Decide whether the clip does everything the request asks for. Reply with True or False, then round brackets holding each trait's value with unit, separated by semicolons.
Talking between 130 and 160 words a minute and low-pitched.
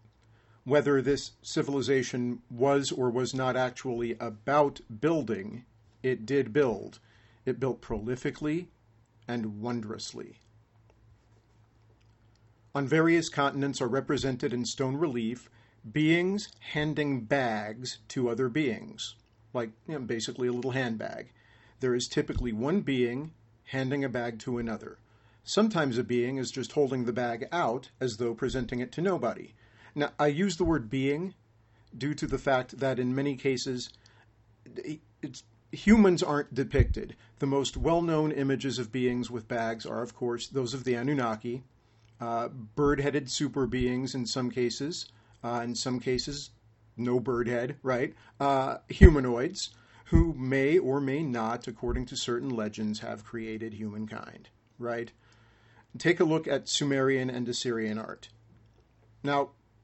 True (140 wpm; 125 Hz)